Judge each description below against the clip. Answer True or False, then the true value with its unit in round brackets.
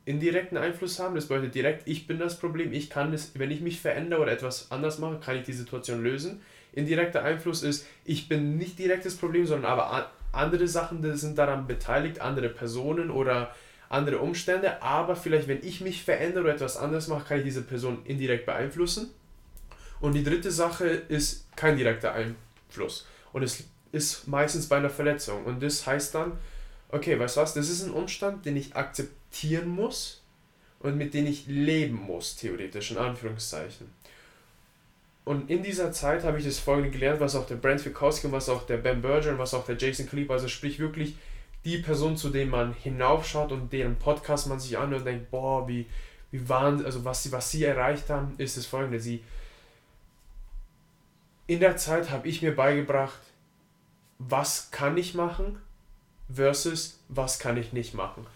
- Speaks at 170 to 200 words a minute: True (185 wpm)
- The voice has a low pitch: False (145 Hz)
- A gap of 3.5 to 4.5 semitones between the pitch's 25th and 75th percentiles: True (3.8 semitones)